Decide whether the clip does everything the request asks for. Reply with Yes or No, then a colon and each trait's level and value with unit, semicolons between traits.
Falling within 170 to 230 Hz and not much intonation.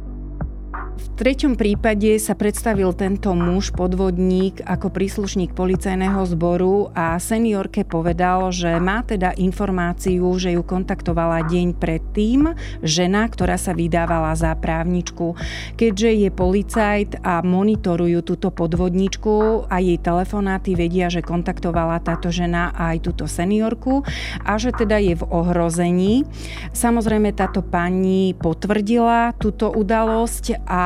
No: medium, 185 Hz; average, 3.3 semitones